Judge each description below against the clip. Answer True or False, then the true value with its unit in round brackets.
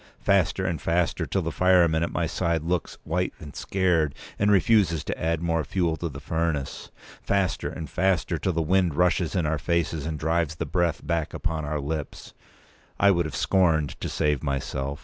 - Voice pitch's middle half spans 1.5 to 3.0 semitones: True (2.6 semitones)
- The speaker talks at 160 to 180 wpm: False (190 wpm)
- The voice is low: True (85 Hz)